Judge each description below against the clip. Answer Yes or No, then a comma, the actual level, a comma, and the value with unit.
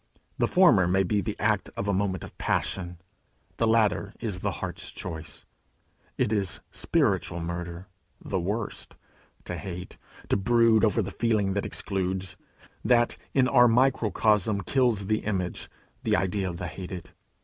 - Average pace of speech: Yes, average, 150 wpm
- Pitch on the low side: Yes, low, 100 Hz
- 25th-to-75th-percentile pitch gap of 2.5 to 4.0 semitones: Yes, average, 3.4 semitones